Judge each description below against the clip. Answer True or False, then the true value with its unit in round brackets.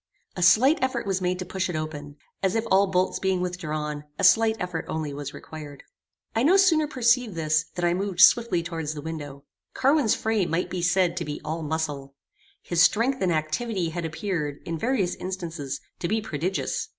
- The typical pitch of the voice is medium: True (175 Hz)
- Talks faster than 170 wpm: True (190 wpm)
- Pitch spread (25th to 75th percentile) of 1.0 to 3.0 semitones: False (4.7 semitones)